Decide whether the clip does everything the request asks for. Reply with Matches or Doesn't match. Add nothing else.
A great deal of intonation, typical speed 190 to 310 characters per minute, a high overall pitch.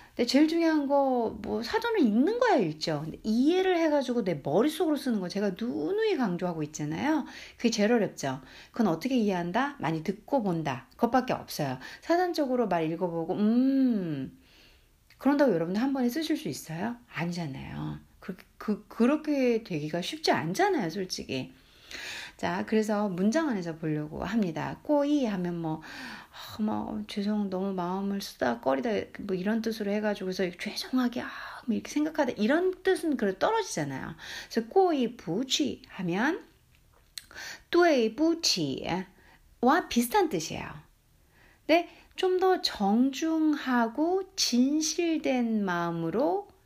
Matches